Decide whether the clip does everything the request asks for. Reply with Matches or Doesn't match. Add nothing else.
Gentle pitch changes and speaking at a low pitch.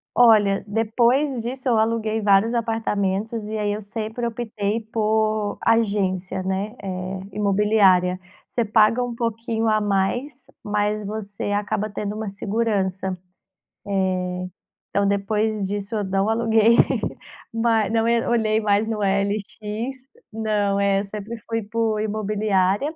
Doesn't match